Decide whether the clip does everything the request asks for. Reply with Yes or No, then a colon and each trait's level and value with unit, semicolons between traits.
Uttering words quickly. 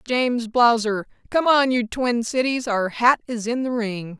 No: average, 160 wpm